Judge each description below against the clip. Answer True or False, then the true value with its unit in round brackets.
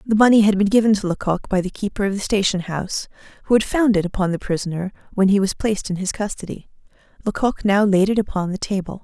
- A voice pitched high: True (200 Hz)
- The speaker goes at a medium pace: False (235 wpm)